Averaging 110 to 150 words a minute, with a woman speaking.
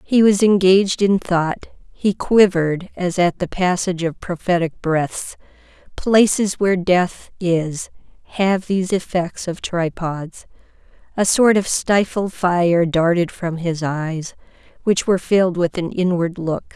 Yes: average, 140 wpm; female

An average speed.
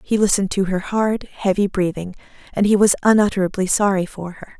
Yes: average, 185 wpm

